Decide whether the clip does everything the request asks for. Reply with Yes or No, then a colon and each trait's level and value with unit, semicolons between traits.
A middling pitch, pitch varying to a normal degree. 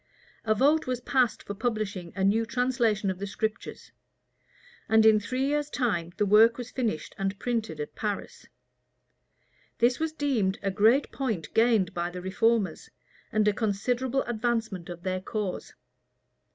No: high, 220 Hz; average, 3.9 semitones